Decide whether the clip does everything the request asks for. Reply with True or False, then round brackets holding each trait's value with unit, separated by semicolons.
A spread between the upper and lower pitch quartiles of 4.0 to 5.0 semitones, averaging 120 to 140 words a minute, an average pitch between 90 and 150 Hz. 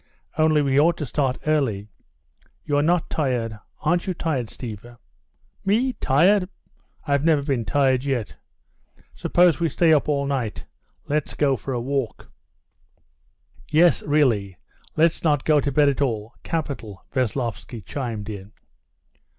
True (4.4 semitones; 135 wpm; 140 Hz)